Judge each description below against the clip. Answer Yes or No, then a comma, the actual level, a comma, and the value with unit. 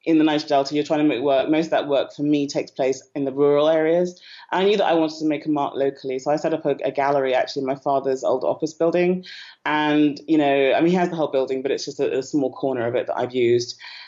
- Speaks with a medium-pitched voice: Yes, medium, 145 Hz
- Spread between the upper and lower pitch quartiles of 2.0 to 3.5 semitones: Yes, narrow, 2.5 semitones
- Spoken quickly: Yes, fast, 280 wpm